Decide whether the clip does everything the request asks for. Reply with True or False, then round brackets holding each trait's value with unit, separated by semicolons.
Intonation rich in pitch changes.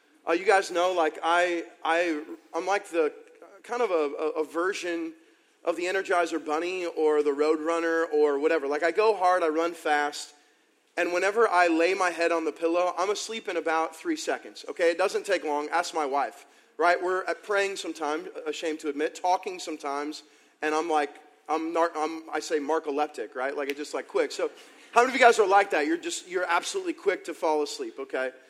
False (3.9 semitones)